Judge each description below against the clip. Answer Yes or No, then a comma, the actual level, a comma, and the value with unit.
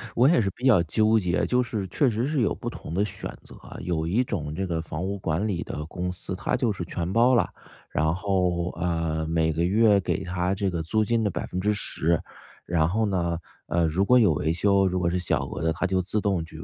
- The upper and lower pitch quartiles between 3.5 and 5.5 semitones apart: Yes, average, 3.9 semitones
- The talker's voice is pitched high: No, very low, 90 Hz